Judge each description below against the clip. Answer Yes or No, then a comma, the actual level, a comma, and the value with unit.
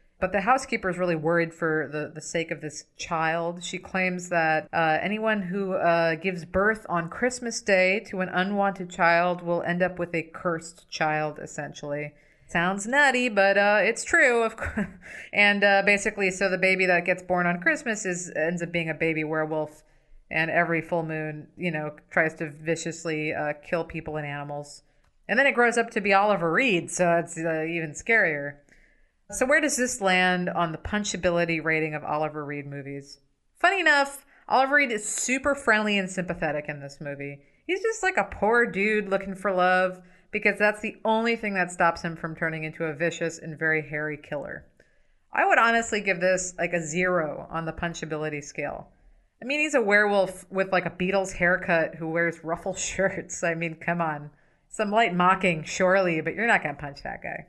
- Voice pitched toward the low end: No, medium, 175 Hz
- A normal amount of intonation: Yes, average, 3.9 semitones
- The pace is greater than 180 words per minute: Yes, average, 190 wpm